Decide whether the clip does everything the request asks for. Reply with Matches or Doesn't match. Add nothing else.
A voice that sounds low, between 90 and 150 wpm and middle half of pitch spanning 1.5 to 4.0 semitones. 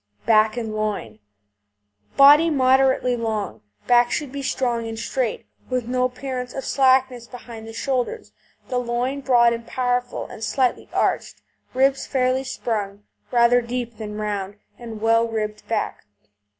Doesn't match